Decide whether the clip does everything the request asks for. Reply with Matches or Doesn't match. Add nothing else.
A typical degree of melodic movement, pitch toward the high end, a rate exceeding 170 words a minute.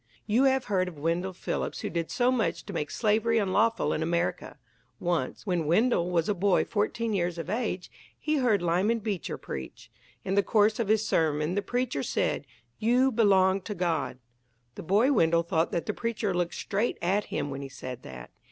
Matches